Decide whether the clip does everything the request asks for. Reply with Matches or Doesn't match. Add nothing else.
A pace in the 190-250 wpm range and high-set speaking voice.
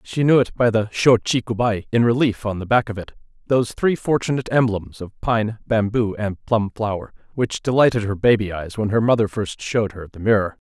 Doesn't match